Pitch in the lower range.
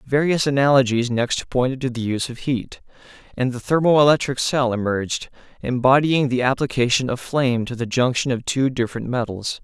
Yes: low, 130 Hz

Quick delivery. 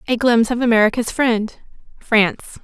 No: slow, 115 wpm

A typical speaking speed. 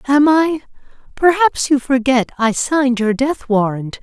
Yes: average, 150 wpm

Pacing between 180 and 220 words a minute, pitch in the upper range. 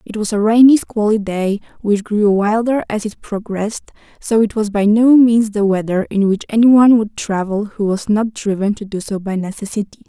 Yes: average, 200 wpm; high, 210 Hz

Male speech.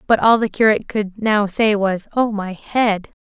No: female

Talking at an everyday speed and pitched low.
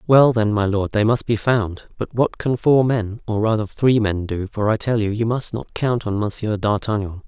No: fast, 230 wpm; low, 110 Hz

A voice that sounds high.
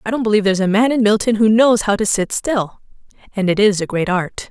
Yes: high, 210 Hz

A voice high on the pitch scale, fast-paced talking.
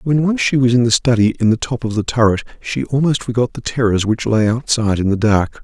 No: low, 115 Hz; fast, 255 wpm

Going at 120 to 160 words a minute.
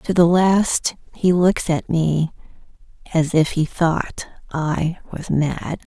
Yes: average, 140 wpm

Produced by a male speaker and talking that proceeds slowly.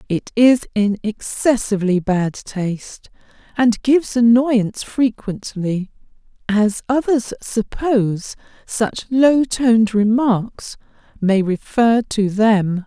No: female; slow, 100 wpm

